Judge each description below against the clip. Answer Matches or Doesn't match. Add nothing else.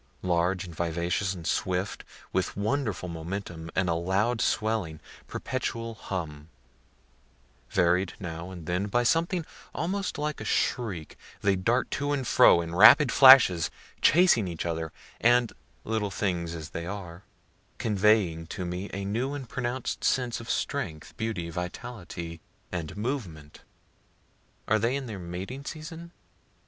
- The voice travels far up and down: Matches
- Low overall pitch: Matches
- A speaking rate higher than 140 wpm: Doesn't match